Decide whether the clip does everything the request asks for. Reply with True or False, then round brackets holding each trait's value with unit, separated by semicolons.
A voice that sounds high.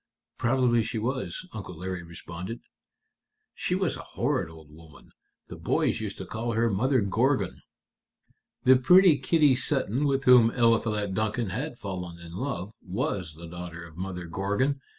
False (110 Hz)